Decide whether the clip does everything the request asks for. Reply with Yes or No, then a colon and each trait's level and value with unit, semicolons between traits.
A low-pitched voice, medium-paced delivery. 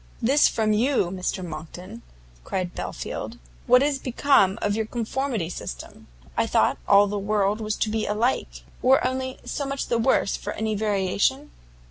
No: high, 215 Hz; average, 160 wpm